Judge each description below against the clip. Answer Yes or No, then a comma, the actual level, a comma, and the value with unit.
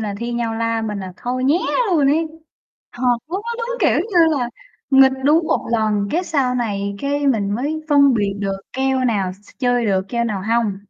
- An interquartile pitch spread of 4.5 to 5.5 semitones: Yes, average, 5.2 semitones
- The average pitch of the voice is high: Yes, high, 245 Hz